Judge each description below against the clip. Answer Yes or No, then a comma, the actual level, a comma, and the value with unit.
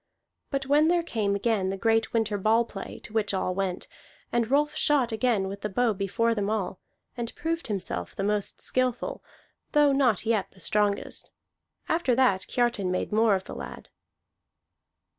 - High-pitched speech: Yes, high, 220 Hz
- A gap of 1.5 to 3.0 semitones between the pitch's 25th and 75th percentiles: No, average, 3.9 semitones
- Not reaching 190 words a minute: Yes, average, 170 wpm